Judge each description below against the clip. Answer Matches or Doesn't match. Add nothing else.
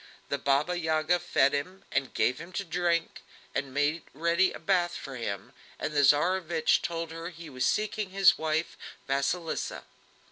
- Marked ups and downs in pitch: Doesn't match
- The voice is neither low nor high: Matches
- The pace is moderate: Matches